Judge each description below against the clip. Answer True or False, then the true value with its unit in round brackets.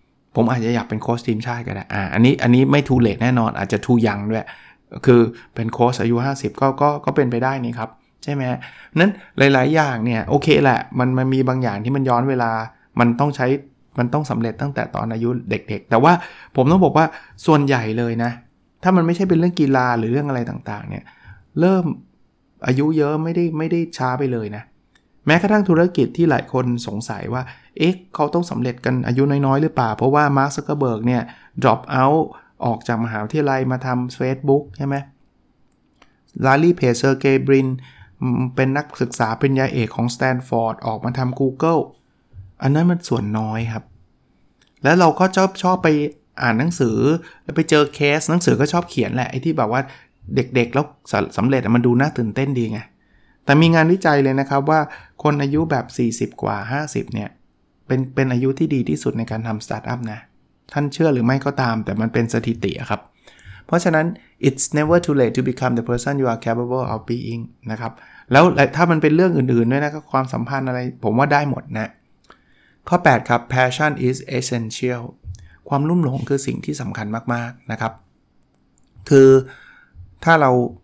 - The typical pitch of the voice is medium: False (130 Hz)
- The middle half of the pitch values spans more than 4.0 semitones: False (3.7 semitones)